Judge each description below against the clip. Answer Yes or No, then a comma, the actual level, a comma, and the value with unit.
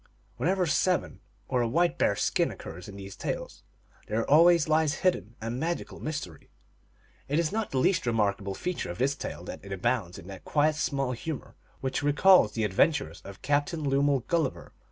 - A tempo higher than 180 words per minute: Yes, average, 190 wpm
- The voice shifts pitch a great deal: Yes, wide, 6.9 semitones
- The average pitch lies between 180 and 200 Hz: No, medium, 140 Hz